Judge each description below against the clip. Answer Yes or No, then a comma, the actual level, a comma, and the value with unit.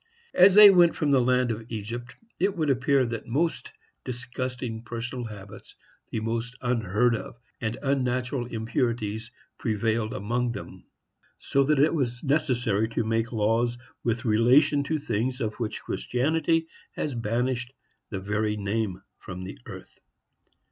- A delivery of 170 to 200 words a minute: No, average, 145 wpm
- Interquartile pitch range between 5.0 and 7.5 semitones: No, average, 2.9 semitones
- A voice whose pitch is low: Yes, low, 120 Hz